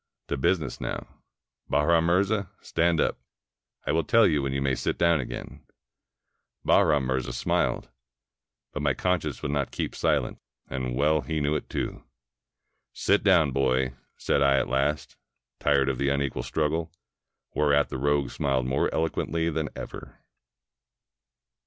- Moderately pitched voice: No, very low, 75 Hz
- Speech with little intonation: No, average, 3.1 semitones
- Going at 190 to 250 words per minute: No, average, 145 wpm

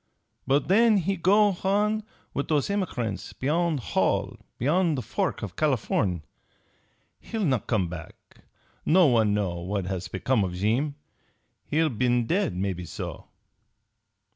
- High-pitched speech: No, low, 135 Hz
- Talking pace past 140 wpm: No, slow, 135 wpm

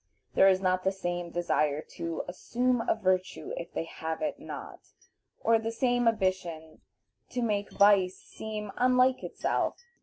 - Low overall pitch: No, high, 195 Hz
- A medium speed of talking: Yes, average, 150 wpm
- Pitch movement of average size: Yes, average, 4.6 semitones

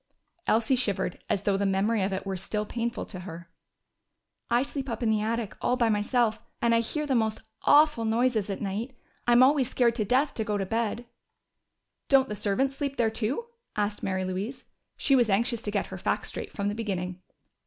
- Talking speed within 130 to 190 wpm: No, fast, 205 wpm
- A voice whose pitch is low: No, high, 220 Hz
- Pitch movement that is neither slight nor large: Yes, average, 3.4 semitones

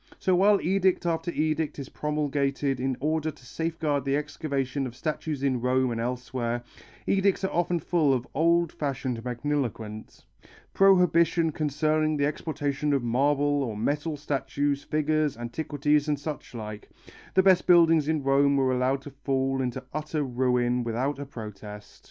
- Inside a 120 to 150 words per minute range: Yes, average, 145 wpm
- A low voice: No, medium, 145 Hz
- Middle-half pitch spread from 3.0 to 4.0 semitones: Yes, average, 3.4 semitones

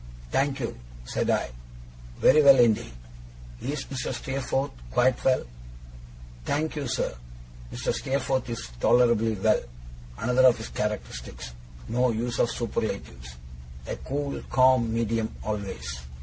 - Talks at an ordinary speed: No, slow, 120 wpm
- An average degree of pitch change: Yes, average, 3.8 semitones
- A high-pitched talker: No, low, 120 Hz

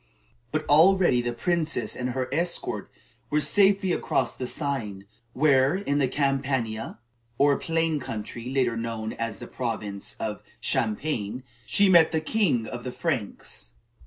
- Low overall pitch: Yes, low, 130 Hz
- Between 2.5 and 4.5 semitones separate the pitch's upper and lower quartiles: No, wide, 5.4 semitones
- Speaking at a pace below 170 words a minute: Yes, average, 140 wpm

